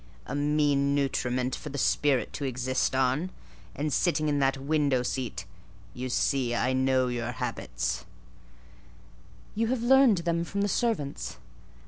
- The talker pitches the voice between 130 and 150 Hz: Yes, medium, 140 Hz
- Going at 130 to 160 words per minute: Yes, average, 140 wpm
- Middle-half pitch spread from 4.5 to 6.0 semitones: No, average, 3.2 semitones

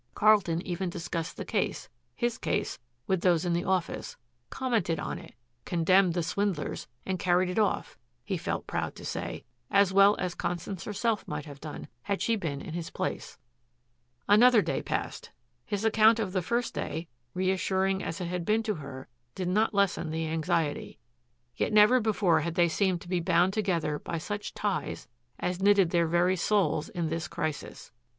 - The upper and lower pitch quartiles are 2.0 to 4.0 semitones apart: Yes, average, 3.4 semitones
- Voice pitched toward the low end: No, medium, 180 Hz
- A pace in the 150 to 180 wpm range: Yes, average, 175 wpm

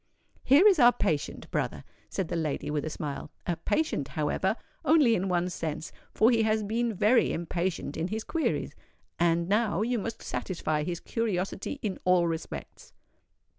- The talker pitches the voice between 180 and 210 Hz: Yes, high, 190 Hz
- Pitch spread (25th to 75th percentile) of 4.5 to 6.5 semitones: Yes, average, 5.3 semitones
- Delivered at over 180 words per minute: No, average, 165 wpm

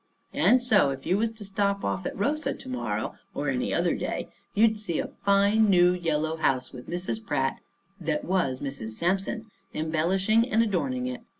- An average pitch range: No, wide, 5.7 semitones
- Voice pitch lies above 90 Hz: Yes, high, 190 Hz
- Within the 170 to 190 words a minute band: Yes, average, 180 wpm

